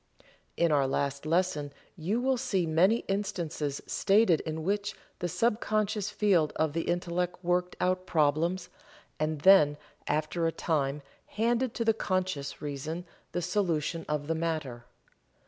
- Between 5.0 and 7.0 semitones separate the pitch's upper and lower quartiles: No, average, 4.2 semitones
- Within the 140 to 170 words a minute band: Yes, average, 145 wpm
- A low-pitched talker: No, medium, 170 Hz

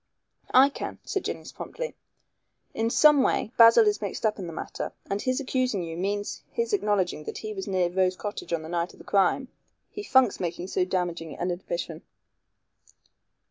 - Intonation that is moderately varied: No, wide, 6.4 semitones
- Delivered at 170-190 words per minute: Yes, average, 180 wpm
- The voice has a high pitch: Yes, high, 200 Hz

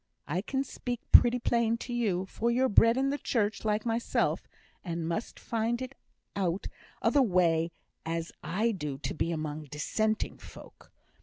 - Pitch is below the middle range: No, high, 215 Hz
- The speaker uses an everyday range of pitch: No, wide, 6.0 semitones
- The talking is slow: No, average, 170 wpm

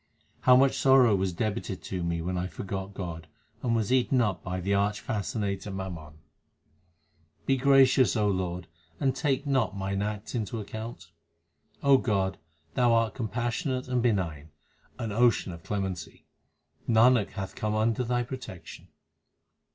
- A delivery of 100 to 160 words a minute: Yes, average, 150 wpm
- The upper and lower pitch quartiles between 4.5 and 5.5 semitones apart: Yes, average, 4.8 semitones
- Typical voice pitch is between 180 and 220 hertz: No, low, 105 Hz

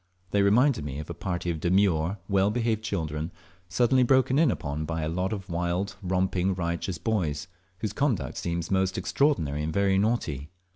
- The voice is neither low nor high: No, very low, 95 Hz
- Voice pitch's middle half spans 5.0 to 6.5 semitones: No, average, 4.4 semitones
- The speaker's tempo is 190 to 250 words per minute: No, average, 180 wpm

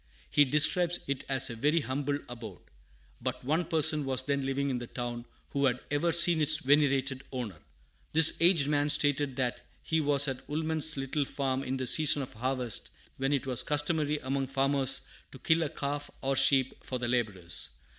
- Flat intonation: Yes, narrow, 2.3 semitones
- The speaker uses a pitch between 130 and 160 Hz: Yes, medium, 140 Hz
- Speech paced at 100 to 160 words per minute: No, average, 185 wpm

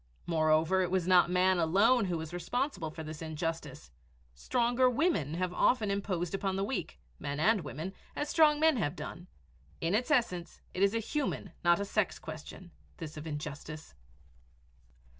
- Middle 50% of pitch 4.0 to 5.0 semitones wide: No, wide, 5.5 semitones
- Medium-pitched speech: Yes, medium, 180 Hz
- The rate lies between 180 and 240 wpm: No, average, 165 wpm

